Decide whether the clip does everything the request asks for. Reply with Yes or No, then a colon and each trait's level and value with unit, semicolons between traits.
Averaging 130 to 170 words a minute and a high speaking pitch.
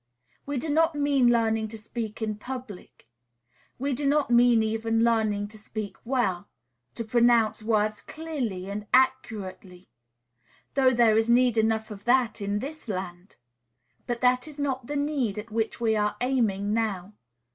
Yes: average, 155 wpm; high, 230 Hz